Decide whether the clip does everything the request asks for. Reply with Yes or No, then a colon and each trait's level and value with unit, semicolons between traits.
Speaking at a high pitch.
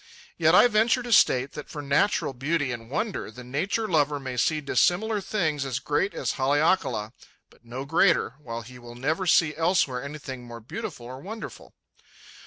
No: medium, 145 Hz